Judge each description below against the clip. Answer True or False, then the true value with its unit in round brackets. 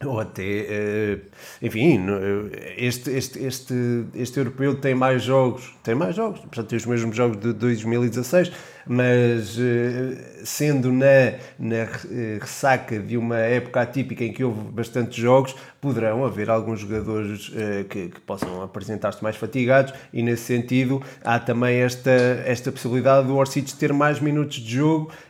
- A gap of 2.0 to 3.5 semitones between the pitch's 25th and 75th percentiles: True (2.8 semitones)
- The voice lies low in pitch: True (125 Hz)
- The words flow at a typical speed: True (140 wpm)